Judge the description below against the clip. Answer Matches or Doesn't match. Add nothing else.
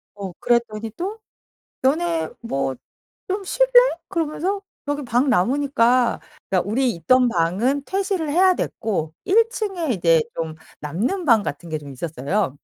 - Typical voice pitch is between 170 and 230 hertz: Doesn't match